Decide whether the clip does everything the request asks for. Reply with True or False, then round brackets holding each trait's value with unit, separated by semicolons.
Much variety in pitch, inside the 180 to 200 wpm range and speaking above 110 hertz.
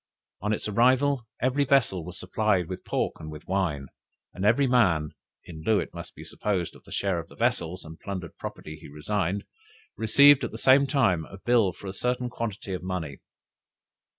False (5.8 semitones; 190 wpm; 100 Hz)